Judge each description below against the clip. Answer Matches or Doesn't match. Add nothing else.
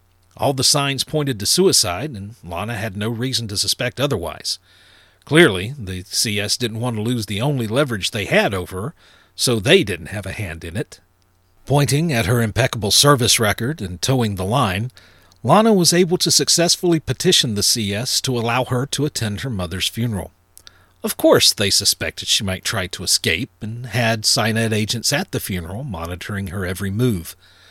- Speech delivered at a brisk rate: Doesn't match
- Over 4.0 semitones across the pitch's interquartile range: Matches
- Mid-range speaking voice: Doesn't match